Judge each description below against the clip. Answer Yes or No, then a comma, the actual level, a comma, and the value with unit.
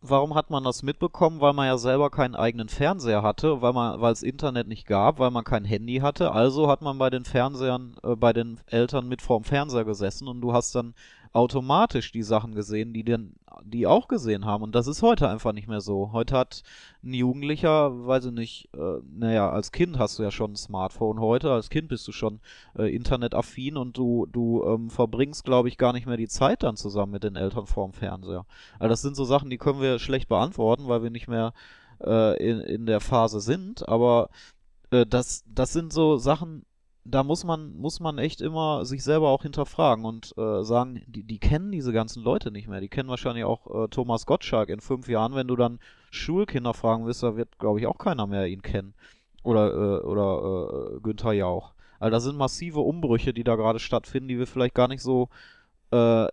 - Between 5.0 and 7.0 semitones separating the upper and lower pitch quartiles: No, average, 3.4 semitones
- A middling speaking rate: No, fast, 215 wpm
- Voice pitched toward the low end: Yes, low, 120 Hz